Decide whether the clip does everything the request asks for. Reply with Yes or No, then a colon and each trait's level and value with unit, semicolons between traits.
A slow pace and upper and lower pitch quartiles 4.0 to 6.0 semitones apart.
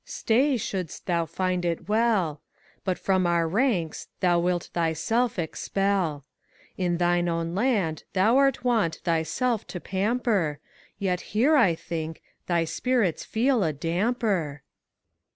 Yes: slow, 130 wpm; average, 5.1 semitones